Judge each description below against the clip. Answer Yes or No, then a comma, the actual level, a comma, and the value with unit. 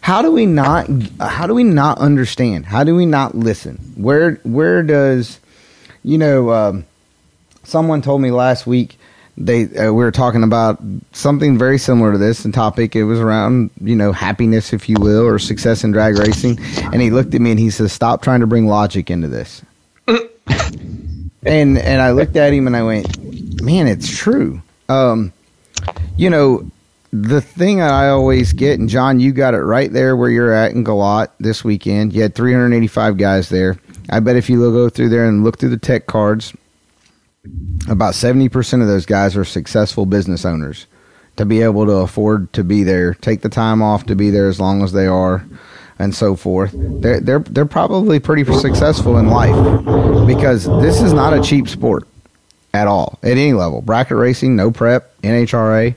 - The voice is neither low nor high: No, low, 110 Hz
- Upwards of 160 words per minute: Yes, average, 190 wpm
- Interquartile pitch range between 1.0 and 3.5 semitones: No, average, 4.1 semitones